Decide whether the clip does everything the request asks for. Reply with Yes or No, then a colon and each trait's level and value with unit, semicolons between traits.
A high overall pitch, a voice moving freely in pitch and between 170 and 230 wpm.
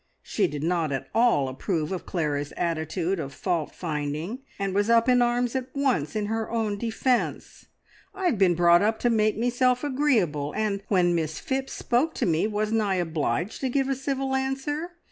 Yes: high, 210 Hz; wide, 6.8 semitones; average, 185 wpm